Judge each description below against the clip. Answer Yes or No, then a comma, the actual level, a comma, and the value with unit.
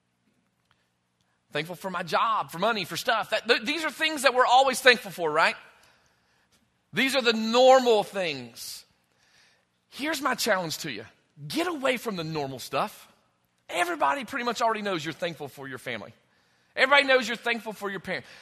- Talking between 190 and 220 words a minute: No, average, 165 wpm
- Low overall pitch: No, high, 195 Hz